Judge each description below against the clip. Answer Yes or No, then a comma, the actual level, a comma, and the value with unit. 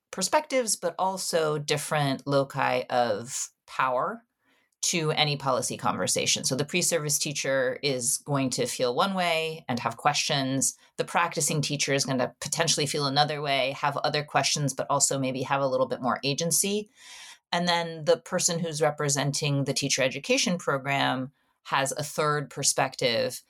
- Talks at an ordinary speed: Yes, average, 155 wpm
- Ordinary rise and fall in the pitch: Yes, average, 3.5 semitones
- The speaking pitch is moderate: Yes, medium, 150 Hz